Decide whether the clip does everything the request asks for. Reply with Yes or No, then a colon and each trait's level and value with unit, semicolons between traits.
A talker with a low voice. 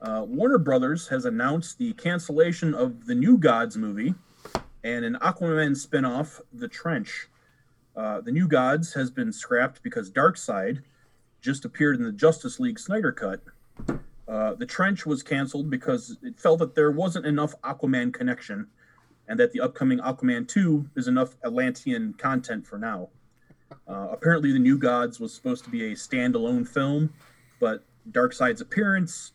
No: medium, 160 Hz